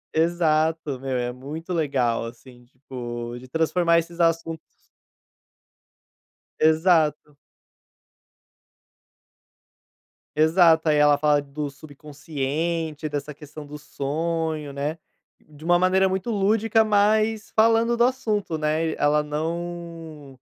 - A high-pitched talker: No, medium, 155 Hz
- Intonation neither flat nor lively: Yes, average, 3.0 semitones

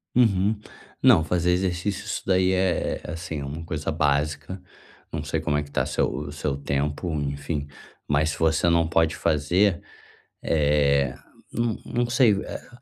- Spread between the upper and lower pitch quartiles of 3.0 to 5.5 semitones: Yes, average, 4.2 semitones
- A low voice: Yes, very low, 80 Hz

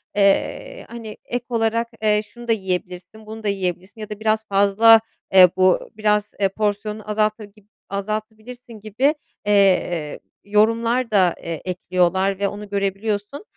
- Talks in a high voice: Yes, high, 210 Hz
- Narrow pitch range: Yes, narrow, 2.1 semitones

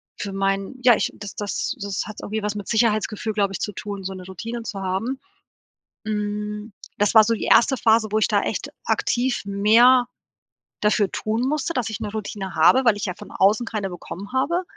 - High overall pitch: Yes, high, 210 Hz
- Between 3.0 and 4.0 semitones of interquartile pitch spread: No, narrow, 2.5 semitones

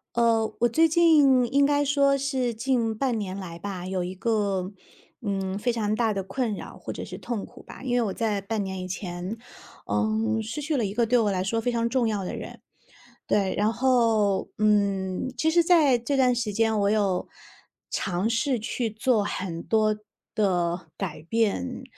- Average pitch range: Yes, average, 4.0 semitones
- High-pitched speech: Yes, high, 220 Hz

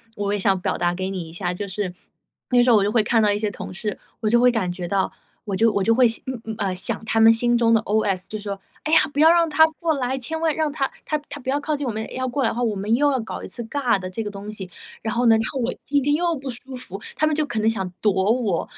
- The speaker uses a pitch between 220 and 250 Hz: Yes, high, 225 Hz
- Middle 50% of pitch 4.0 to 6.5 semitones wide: Yes, average, 4.6 semitones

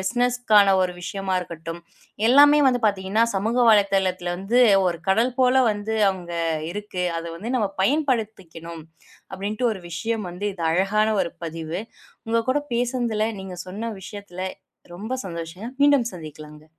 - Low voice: No, high, 200 Hz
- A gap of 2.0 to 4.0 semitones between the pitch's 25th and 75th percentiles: No, average, 4.6 semitones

